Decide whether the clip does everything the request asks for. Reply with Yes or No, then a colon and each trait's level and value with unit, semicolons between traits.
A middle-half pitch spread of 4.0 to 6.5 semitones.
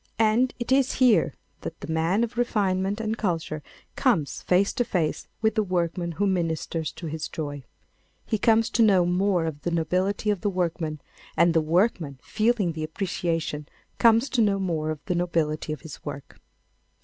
Yes: average, 4.9 semitones